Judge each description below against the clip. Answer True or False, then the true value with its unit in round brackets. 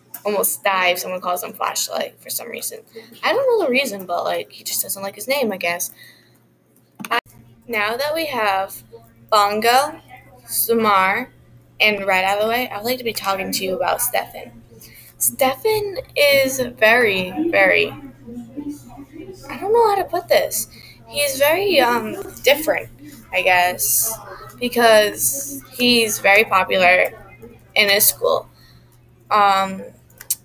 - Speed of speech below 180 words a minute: True (140 wpm)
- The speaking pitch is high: True (215 Hz)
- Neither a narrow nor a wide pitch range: False (6.9 semitones)